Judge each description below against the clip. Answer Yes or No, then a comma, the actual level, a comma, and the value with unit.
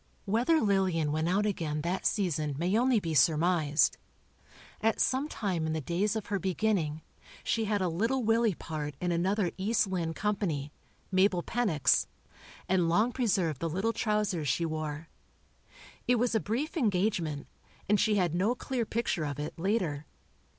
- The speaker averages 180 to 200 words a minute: No, average, 155 wpm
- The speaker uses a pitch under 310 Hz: Yes, medium, 185 Hz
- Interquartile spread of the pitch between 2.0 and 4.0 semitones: No, average, 5.3 semitones